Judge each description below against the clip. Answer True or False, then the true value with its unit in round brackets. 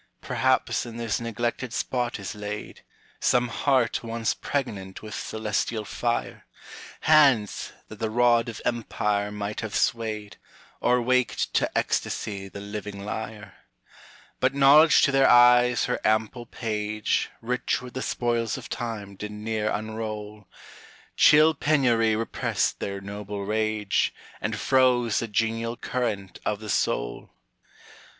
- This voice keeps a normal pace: False (130 wpm)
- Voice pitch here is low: True (110 Hz)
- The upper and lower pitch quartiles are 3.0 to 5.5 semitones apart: False (2.6 semitones)